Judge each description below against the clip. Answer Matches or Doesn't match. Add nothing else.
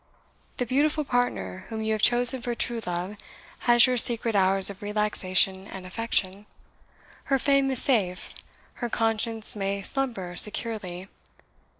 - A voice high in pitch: Matches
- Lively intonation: Doesn't match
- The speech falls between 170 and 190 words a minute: Doesn't match